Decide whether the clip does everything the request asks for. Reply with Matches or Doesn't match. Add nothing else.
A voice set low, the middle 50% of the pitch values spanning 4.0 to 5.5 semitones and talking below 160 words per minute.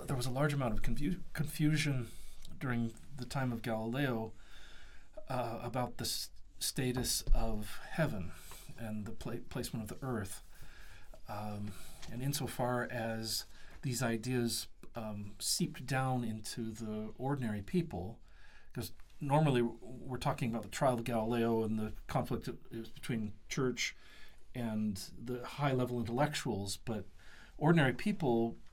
Doesn't match